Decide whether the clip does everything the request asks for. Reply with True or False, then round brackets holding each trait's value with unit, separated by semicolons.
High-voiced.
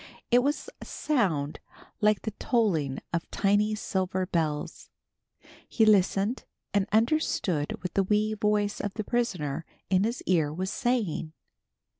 True (200 Hz)